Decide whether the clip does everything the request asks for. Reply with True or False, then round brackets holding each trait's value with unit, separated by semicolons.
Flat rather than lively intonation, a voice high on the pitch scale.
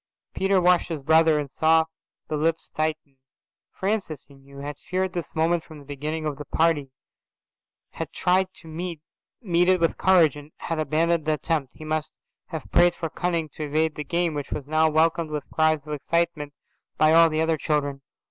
False (2.0 semitones; 160 Hz)